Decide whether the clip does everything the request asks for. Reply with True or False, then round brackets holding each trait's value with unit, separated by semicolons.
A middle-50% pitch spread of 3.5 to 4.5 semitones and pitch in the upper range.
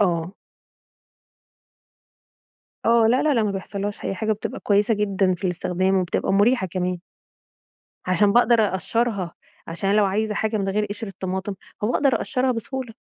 False (2.9 semitones; 205 Hz)